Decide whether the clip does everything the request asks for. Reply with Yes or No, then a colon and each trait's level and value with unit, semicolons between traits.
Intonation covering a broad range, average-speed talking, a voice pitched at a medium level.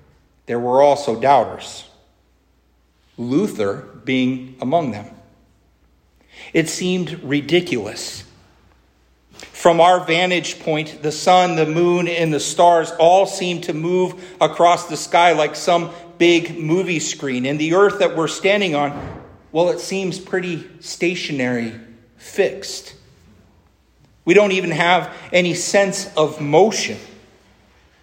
No: wide, 6.1 semitones; slow, 120 wpm; medium, 160 Hz